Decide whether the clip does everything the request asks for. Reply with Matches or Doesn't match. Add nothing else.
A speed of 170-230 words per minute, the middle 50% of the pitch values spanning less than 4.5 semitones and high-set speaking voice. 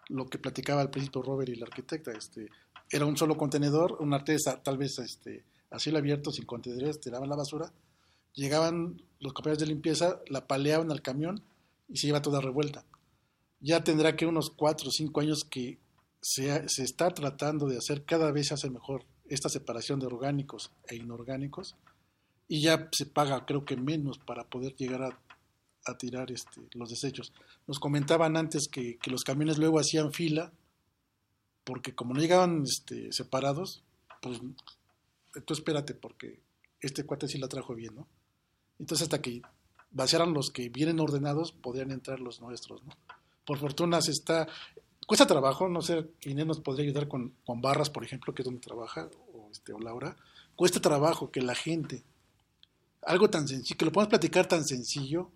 Doesn't match